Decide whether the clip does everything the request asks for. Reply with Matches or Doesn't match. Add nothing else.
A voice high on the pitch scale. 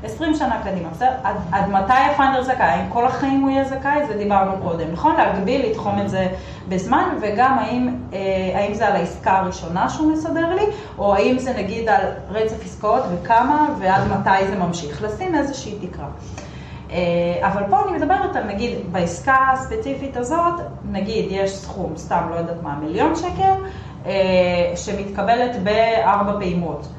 Matches